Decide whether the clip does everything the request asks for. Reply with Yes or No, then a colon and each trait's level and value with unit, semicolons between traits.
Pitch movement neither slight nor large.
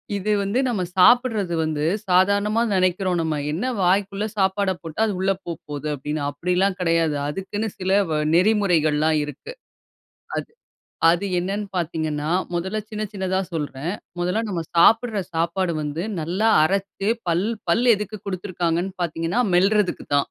Yes: average, 3.5 semitones